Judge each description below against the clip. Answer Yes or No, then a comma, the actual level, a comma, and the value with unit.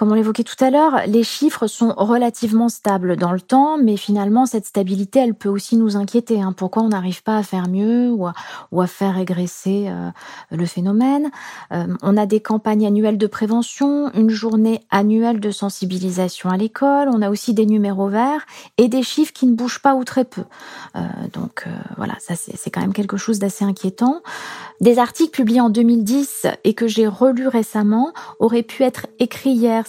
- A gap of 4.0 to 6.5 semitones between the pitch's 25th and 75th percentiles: No, average, 3.5 semitones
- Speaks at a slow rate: No, average, 195 wpm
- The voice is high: Yes, high, 220 Hz